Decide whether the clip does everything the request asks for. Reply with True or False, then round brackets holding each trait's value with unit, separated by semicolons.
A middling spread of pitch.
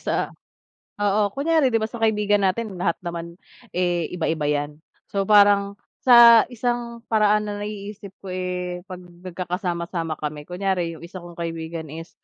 True (3.6 semitones)